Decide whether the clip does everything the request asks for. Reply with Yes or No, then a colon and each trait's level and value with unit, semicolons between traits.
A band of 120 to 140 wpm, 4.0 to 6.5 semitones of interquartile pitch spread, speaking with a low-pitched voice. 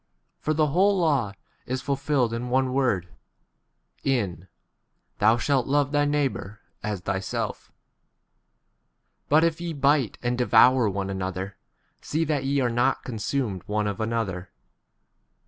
Yes: slow, 135 wpm; wide, 5.5 semitones; low, 125 Hz